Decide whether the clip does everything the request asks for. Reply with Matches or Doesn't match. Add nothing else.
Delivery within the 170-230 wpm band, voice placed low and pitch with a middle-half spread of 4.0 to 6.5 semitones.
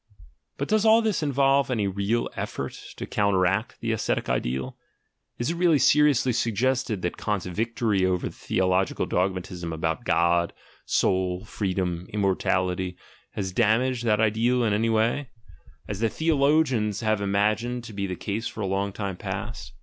Doesn't match